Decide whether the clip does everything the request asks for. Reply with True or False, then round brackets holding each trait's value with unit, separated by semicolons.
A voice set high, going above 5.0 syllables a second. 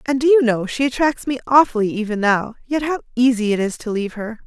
True (240 Hz; 6.0 syllables/s)